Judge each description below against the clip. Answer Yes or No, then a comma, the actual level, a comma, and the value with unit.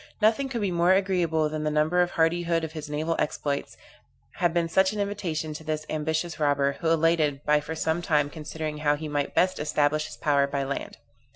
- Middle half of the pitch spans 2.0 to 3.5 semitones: Yes, narrow, 2.5 semitones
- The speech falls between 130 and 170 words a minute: No, fast, 205 wpm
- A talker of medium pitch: Yes, medium, 160 Hz